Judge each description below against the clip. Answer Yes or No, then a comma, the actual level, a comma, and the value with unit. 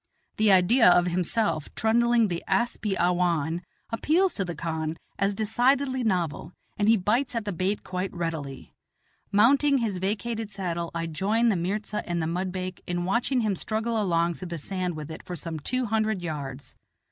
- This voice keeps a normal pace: Yes, average, 175 wpm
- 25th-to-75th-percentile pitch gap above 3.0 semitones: Yes, average, 4.6 semitones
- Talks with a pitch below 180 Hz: No, high, 190 Hz